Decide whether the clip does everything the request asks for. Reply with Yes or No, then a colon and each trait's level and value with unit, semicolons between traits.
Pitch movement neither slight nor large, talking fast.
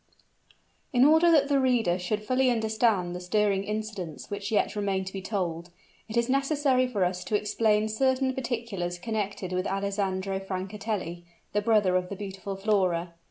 No: average, 3.6 semitones; average, 160 wpm